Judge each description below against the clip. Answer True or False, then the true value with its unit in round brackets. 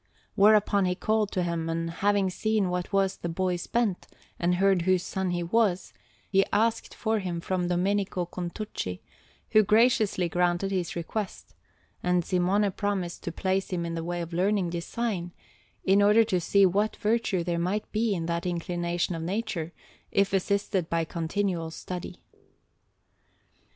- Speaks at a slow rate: False (155 wpm)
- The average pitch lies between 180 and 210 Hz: True (185 Hz)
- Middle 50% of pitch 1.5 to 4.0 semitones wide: True (2.8 semitones)